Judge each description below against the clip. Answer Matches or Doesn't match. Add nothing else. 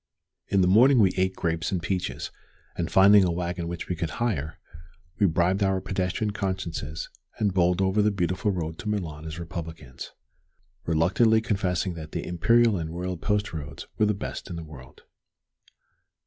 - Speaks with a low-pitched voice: Matches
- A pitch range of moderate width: Matches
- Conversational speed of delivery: Matches